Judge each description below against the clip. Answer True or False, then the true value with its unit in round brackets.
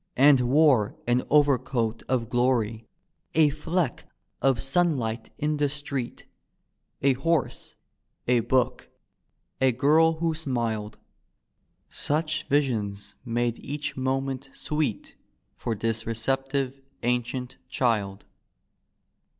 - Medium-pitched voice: False (130 Hz)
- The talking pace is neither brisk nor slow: False (100 wpm)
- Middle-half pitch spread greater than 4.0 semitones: False (3.7 semitones)